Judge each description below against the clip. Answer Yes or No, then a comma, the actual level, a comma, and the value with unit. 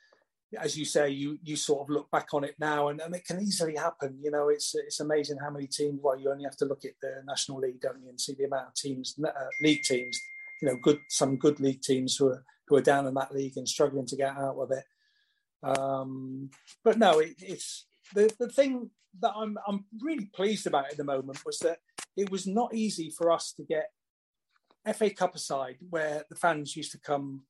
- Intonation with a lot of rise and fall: Yes, wide, 6.6 semitones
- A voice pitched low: No, medium, 150 Hz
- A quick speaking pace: Yes, fast, 230 wpm